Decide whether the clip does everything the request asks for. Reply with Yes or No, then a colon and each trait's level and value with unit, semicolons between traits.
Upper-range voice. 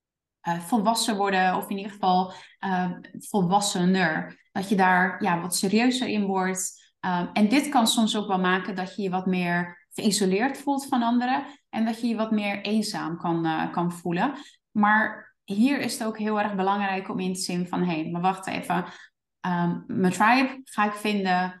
Yes: high, 200 Hz